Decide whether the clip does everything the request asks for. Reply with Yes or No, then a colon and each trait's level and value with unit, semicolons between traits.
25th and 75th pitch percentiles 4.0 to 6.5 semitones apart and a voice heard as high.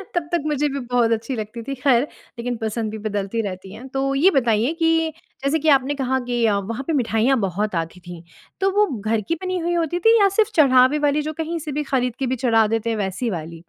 Yes: wide, 5.6 semitones; very high, 250 Hz